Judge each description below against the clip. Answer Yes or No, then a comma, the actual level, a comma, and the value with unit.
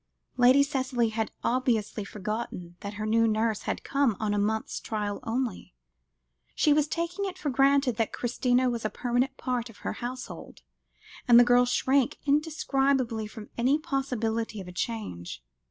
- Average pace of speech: Yes, average, 160 wpm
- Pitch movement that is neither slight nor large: Yes, average, 3.6 semitones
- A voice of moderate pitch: No, high, 240 Hz